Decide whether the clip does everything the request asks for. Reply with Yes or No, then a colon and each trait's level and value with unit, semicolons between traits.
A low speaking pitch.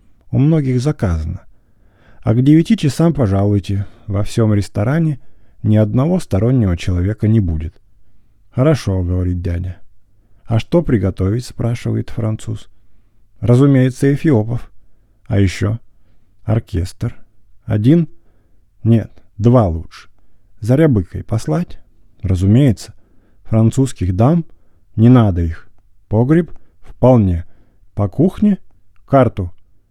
Yes: low, 105 Hz